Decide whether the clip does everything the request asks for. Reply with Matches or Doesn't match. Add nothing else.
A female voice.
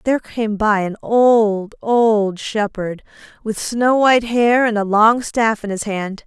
Matches